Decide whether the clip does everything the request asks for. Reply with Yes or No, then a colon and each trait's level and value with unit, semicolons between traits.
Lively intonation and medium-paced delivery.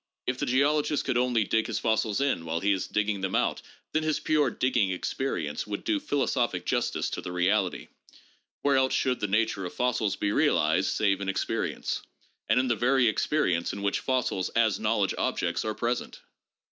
No: average, 4.9 semitones; average, 190 wpm